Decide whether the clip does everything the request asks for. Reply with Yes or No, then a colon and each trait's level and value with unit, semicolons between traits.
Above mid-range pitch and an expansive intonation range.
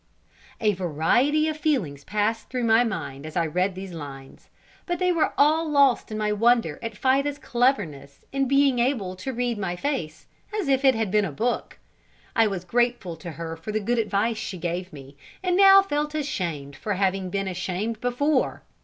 Yes: high, 215 Hz; wide, 7.1 semitones